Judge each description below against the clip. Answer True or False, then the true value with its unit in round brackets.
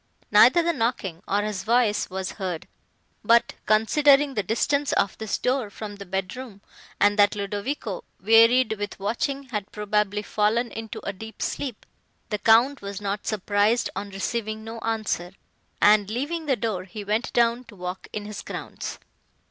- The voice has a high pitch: True (215 Hz)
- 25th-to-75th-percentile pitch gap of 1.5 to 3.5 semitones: True (2.7 semitones)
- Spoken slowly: False (160 wpm)